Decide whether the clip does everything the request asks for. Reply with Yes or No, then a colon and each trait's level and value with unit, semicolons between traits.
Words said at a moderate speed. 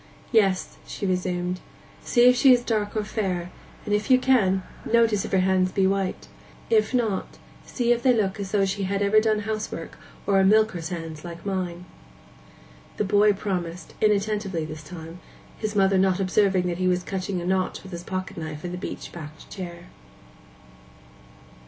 Yes: average, 180 wpm